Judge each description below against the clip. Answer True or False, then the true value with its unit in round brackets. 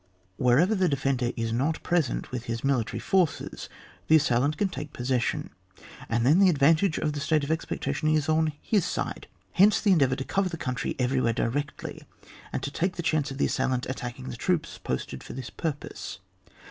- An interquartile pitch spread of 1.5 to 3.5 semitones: False (4.1 semitones)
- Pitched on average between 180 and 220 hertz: False (145 Hz)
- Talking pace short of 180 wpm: False (185 wpm)